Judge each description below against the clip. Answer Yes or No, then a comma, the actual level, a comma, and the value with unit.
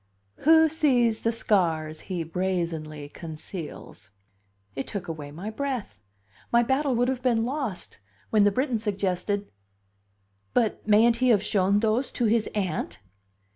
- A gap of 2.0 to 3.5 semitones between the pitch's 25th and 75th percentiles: No, wide, 5.4 semitones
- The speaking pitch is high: Yes, high, 210 Hz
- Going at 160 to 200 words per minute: No, slow, 135 wpm